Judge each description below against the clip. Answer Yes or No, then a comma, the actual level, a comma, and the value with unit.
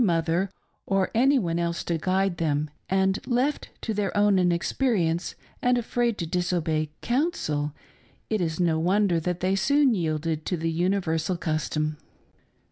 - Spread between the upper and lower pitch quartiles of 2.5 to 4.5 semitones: Yes, average, 4.0 semitones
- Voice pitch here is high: No, medium, 180 Hz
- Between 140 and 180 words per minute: Yes, average, 150 wpm